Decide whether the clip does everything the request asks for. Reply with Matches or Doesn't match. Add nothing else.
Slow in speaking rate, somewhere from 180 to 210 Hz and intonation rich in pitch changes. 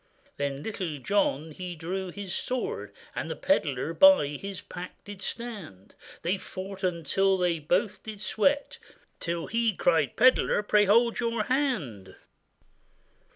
Doesn't match